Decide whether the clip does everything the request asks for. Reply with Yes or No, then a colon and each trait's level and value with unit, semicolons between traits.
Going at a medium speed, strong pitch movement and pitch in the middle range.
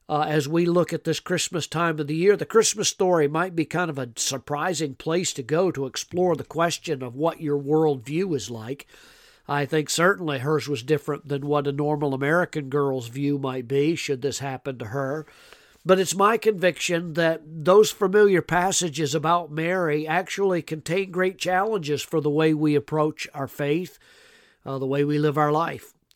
No: average, 190 wpm; average, 3.7 semitones; medium, 155 Hz